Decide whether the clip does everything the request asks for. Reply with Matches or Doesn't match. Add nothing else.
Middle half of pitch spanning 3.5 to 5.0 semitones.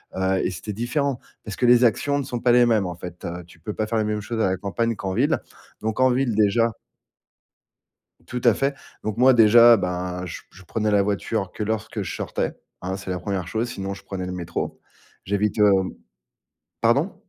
Matches